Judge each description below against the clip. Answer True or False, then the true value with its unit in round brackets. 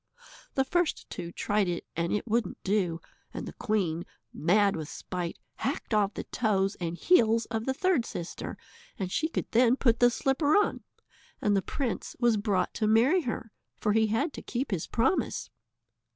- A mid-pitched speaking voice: False (220 Hz)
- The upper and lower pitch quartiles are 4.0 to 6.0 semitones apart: True (4.3 semitones)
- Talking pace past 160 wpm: True (180 wpm)